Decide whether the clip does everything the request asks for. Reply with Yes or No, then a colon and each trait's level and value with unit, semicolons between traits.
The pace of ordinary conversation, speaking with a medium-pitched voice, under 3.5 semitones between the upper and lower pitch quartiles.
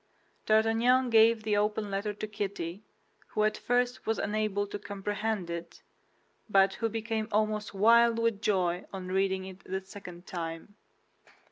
No: average, 145 wpm; high, 210 Hz; narrow, 2.4 semitones